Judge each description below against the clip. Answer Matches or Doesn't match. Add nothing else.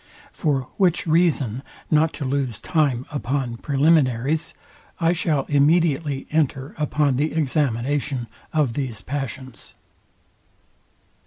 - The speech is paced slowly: Matches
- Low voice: Doesn't match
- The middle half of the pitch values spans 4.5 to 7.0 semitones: Doesn't match